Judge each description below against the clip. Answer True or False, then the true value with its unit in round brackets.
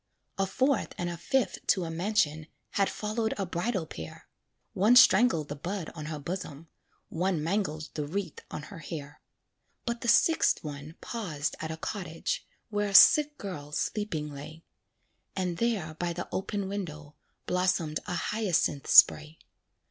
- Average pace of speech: True (155 wpm)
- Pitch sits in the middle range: True (175 Hz)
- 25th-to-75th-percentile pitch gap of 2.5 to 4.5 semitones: False (4.9 semitones)